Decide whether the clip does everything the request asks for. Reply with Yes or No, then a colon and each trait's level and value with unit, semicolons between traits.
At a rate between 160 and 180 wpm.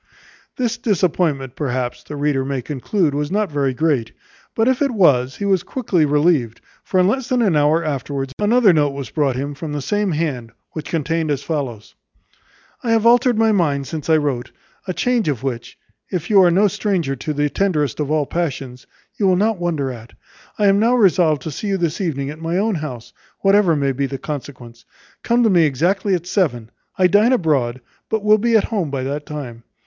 No: fast, 205 wpm